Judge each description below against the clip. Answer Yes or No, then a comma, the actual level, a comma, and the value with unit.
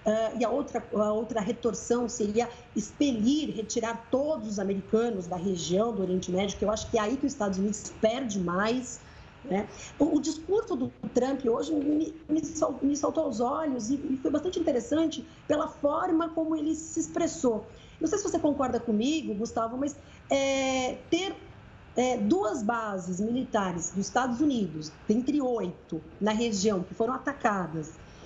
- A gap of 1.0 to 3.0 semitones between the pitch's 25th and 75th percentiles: No, wide, 5.4 semitones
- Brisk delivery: No, average, 170 wpm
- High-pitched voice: Yes, high, 245 Hz